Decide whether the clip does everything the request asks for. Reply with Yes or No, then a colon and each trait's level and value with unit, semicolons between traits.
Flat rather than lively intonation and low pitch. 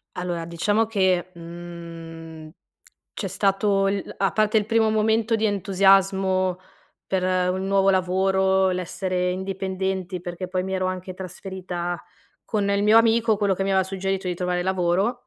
No: narrow, 1.6 semitones; high, 190 Hz